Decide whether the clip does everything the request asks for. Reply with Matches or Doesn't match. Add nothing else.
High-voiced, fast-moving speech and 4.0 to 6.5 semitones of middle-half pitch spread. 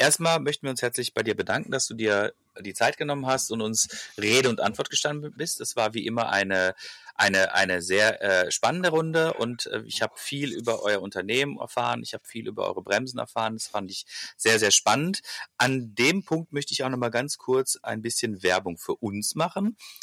Doesn't match